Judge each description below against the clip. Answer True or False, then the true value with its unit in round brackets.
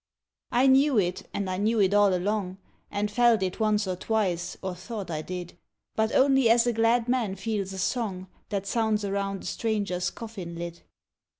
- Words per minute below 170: False (190 wpm)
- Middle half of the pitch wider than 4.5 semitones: False (3.5 semitones)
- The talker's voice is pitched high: True (205 Hz)